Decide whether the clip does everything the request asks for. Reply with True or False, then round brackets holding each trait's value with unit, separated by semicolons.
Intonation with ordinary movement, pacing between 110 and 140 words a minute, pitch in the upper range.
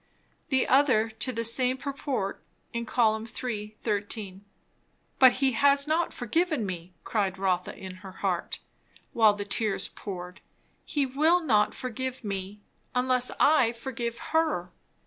True (4.5 semitones; 135 wpm; 230 Hz)